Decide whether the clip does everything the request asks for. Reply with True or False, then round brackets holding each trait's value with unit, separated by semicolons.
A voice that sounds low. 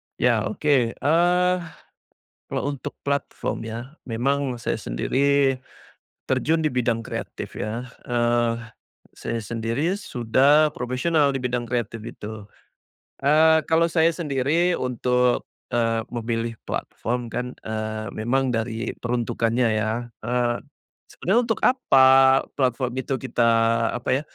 True (125 Hz)